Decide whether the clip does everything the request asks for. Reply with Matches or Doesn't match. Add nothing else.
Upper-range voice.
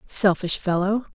Matches